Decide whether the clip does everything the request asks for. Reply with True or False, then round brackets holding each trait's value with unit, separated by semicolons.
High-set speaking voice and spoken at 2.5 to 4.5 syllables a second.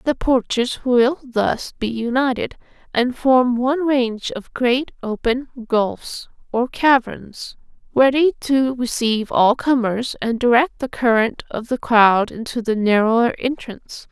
True (245 Hz; 4.0 syllables/s)